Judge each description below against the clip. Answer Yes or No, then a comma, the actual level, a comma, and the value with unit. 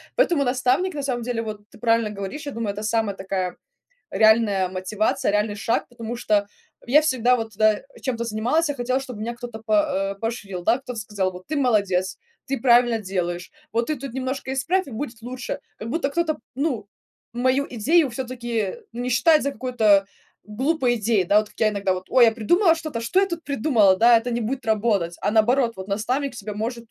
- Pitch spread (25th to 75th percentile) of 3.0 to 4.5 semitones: Yes, average, 3.7 semitones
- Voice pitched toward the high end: Yes, high, 235 Hz